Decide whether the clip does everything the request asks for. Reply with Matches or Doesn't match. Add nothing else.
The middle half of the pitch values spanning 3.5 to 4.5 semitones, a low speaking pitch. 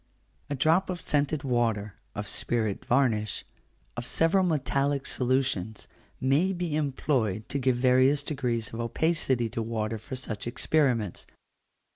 Matches